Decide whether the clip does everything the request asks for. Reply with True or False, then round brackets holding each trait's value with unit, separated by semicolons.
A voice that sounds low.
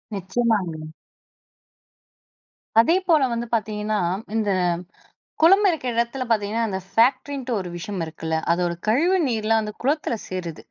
False (225 Hz)